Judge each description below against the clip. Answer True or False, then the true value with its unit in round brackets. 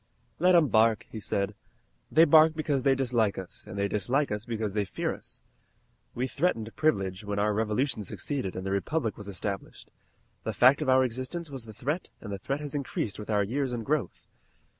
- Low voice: True (115 Hz)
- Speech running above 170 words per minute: True (200 wpm)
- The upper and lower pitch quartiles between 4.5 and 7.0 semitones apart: True (5.4 semitones)